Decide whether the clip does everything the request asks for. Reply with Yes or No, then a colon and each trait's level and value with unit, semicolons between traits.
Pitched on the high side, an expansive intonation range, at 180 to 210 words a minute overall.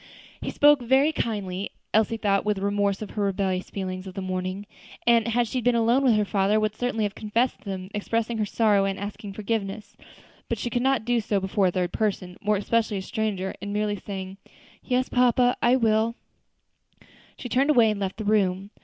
No: high, 210 Hz; average, 2.9 semitones; average, 200 wpm